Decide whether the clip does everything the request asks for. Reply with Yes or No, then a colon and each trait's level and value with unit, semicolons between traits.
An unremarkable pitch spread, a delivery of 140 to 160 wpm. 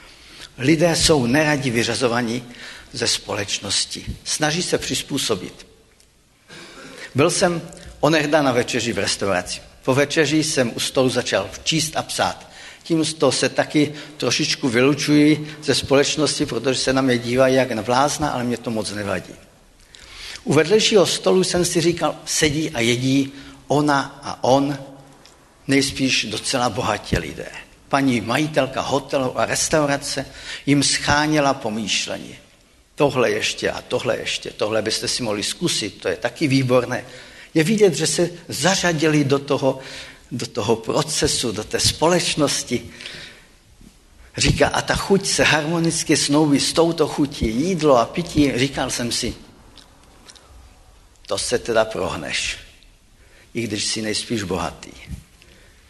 No: average, 4.2 semitones; average, 130 wpm